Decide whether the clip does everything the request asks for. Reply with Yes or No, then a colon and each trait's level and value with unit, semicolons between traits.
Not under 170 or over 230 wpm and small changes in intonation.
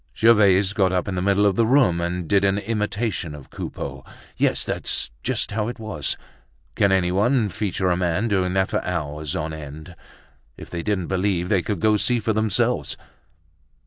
No: average, 180 wpm; average, 3.1 semitones